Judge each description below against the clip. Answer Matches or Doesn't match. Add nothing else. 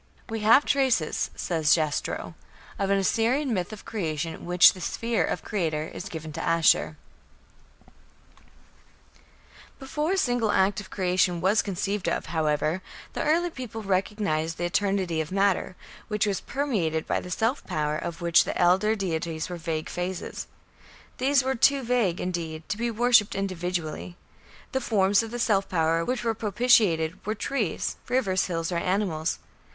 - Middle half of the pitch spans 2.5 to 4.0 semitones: Doesn't match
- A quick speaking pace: Doesn't match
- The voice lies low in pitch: Doesn't match